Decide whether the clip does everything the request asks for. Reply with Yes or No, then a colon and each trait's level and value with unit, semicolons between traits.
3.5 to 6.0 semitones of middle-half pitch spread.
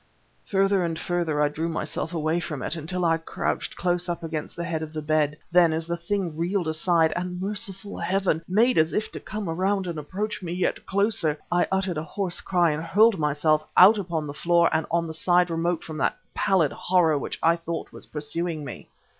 No: average, 2.7 semitones